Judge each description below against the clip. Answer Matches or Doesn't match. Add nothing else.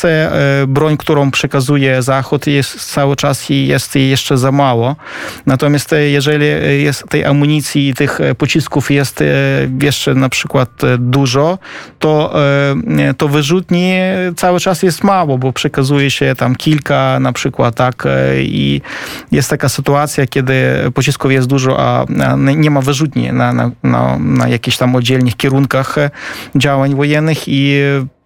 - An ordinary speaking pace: Matches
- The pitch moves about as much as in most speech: Doesn't match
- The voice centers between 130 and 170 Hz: Matches